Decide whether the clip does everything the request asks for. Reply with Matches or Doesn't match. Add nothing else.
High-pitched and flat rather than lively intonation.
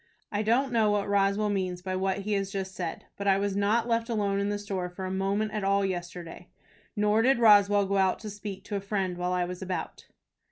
Matches